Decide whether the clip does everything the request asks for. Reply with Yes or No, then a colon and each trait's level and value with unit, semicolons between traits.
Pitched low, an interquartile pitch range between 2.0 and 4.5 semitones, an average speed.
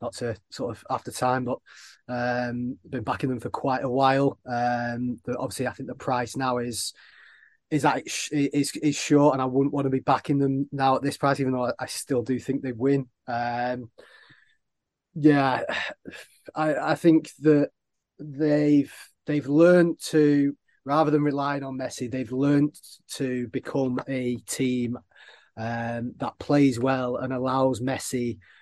Yes: low, 130 Hz; narrow, 2.4 semitones; average, 170 wpm